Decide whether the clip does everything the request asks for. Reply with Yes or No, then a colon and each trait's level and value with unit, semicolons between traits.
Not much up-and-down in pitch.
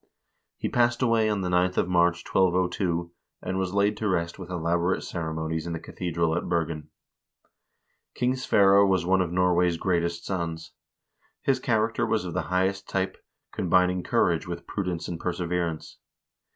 Yes: narrow, 1.8 semitones